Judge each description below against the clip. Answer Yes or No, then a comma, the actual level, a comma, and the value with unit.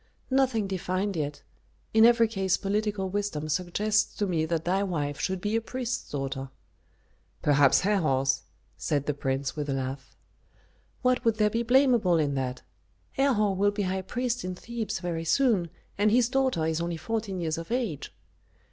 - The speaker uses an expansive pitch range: Yes, wide, 6.1 semitones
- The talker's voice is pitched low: No, high, 190 Hz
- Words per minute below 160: No, average, 165 wpm